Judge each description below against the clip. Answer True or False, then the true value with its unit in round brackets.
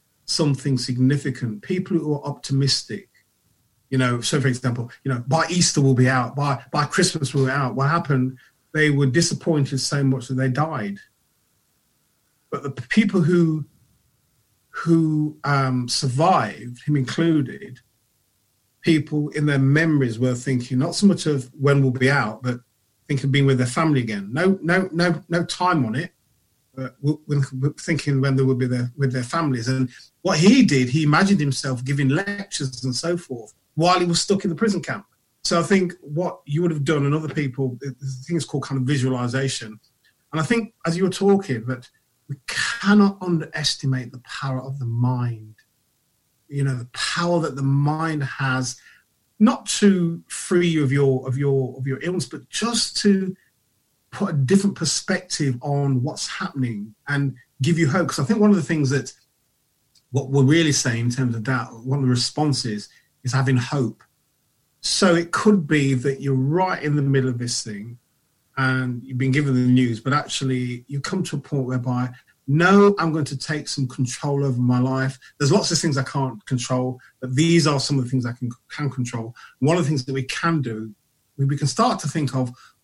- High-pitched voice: False (140 Hz)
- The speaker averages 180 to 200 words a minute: True (190 wpm)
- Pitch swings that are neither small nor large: True (4.0 semitones)